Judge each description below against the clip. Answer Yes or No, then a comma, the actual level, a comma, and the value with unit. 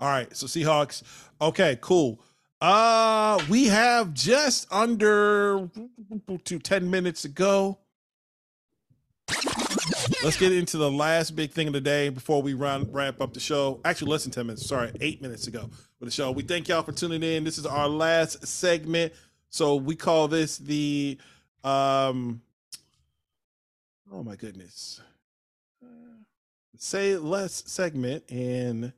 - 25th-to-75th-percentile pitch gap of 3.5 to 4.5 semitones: No, wide, 5.6 semitones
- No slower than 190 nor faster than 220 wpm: No, average, 140 wpm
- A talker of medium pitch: Yes, medium, 155 Hz